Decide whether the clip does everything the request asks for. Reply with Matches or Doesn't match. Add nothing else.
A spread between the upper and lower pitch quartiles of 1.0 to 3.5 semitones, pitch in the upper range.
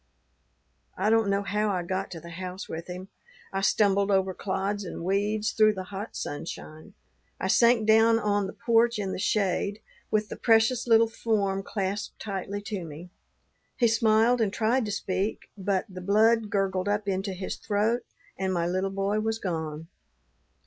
Matches